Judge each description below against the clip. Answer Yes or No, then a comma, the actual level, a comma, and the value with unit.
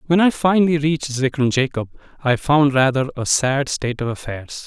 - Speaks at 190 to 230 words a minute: No, average, 180 wpm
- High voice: No, medium, 140 Hz